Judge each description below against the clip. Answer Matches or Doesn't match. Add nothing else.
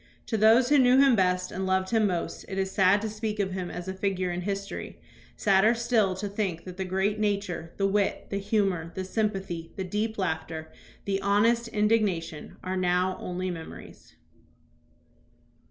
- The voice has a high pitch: Matches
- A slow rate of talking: Doesn't match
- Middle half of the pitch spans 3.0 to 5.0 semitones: Doesn't match